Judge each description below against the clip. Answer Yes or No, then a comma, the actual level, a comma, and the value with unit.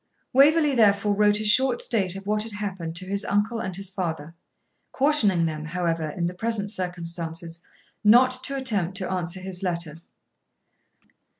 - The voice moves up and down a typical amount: Yes, average, 3.9 semitones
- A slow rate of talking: No, average, 160 wpm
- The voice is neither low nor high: No, high, 195 Hz